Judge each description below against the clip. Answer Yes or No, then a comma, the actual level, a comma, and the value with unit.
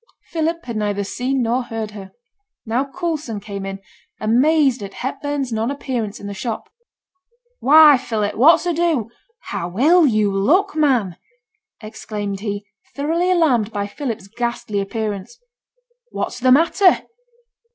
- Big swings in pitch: Yes, wide, 6.2 semitones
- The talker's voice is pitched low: No, high, 240 Hz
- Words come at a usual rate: No, slow, 130 wpm